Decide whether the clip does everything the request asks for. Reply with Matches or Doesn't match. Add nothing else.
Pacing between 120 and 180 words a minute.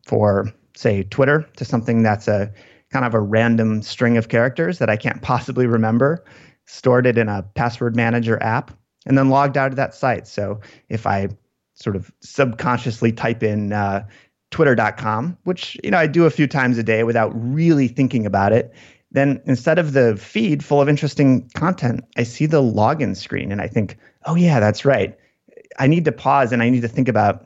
Doesn't match